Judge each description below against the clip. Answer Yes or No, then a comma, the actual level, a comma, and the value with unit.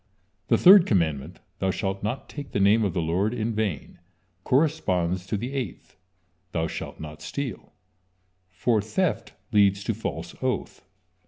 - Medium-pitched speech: No, low, 100 Hz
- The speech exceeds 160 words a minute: No, average, 150 wpm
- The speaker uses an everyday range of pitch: Yes, average, 4.8 semitones